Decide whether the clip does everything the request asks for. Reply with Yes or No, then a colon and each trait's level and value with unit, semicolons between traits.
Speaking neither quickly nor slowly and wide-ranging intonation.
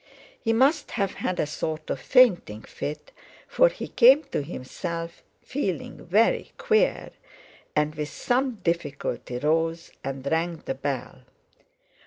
No: slow, 130 wpm; wide, 8.4 semitones